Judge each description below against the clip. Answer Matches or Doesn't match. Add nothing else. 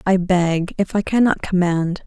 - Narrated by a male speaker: Doesn't match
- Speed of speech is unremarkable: Matches